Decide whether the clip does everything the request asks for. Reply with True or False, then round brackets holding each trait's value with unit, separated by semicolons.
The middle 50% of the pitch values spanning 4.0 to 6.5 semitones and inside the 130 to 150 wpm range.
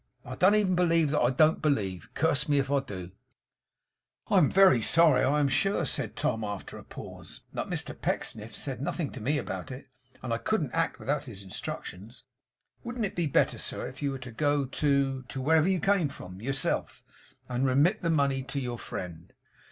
False (4.4 semitones; 200 wpm)